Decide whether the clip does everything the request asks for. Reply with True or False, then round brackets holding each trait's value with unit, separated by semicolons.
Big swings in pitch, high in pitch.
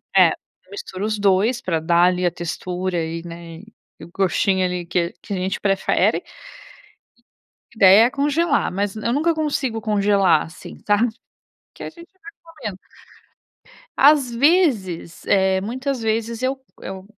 True (6.0 semitones; 200 Hz)